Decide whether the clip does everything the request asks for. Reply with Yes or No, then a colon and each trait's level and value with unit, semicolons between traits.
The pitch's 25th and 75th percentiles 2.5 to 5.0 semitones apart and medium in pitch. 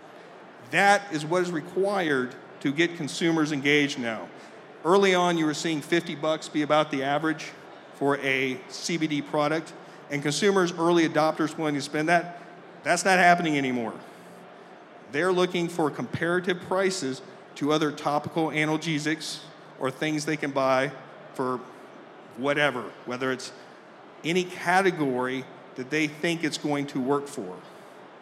Yes: average, 3.4 semitones; medium, 155 Hz